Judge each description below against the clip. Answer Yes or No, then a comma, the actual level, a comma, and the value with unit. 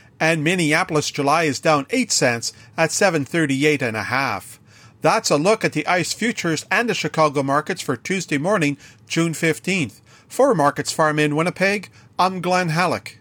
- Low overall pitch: No, medium, 155 Hz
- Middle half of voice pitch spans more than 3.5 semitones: Yes, average, 4.2 semitones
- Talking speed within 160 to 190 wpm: Yes, average, 165 wpm